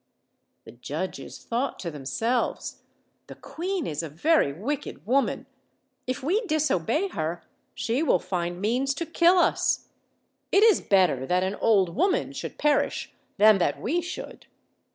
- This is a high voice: Yes, high, 230 Hz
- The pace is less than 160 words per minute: Yes, average, 145 wpm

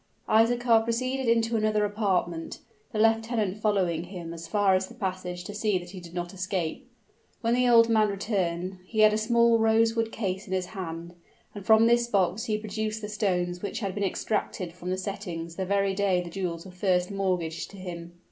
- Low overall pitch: No, high, 200 Hz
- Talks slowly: No, average, 195 wpm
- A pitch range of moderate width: Yes, average, 3.7 semitones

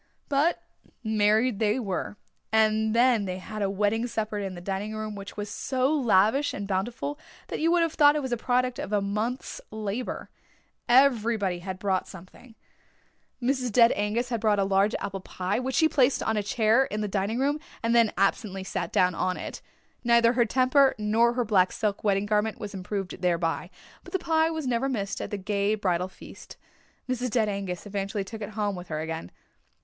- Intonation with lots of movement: No, average, 3.8 semitones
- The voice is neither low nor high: No, high, 215 Hz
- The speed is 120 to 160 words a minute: No, average, 195 wpm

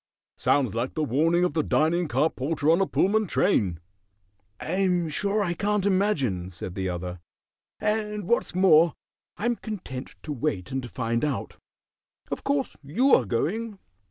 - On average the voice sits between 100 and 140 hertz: No, medium, 165 Hz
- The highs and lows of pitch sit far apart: Yes, wide, 7.8 semitones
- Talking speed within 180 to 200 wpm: No, average, 155 wpm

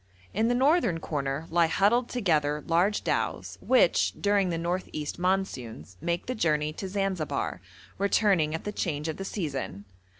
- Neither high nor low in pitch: Yes, medium, 175 Hz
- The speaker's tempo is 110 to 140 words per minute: No, average, 160 wpm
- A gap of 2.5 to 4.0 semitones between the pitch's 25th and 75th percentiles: No, average, 4.9 semitones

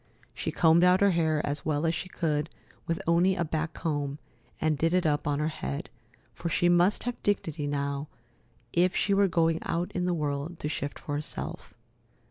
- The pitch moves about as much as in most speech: Yes, average, 3.0 semitones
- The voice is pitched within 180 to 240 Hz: No, medium, 160 Hz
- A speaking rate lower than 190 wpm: No, average, 195 wpm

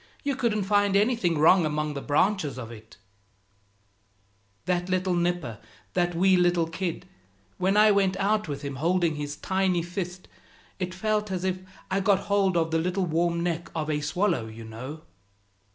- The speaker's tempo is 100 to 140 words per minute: No, average, 170 wpm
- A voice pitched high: No, medium, 175 Hz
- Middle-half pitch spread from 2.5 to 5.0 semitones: Yes, average, 4.3 semitones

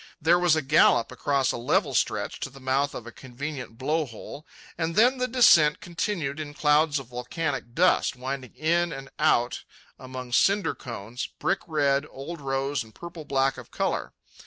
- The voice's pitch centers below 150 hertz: Yes, medium, 140 Hz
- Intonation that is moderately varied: Yes, average, 3.9 semitones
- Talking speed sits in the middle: Yes, average, 175 wpm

